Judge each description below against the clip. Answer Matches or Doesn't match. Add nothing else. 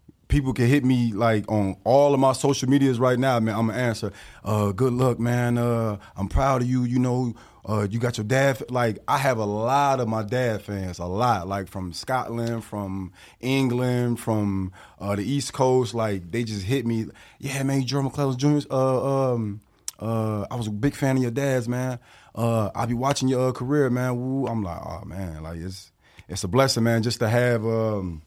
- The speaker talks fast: Matches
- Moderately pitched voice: Doesn't match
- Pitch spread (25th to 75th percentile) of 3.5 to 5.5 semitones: Matches